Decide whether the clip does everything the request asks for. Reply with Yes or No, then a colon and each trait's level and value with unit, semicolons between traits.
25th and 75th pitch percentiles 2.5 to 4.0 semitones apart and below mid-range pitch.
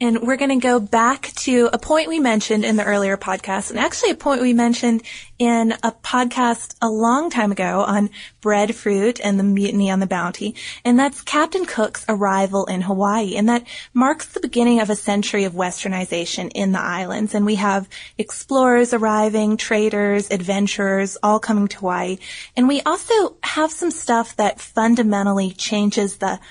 No: average, 3.3 semitones; high, 215 Hz